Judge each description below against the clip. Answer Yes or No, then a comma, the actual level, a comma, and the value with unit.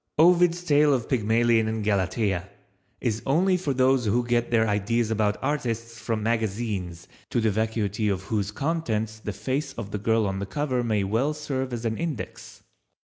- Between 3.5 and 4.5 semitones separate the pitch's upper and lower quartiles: Yes, average, 4.0 semitones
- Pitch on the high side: No, low, 115 Hz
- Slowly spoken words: No, average, 175 wpm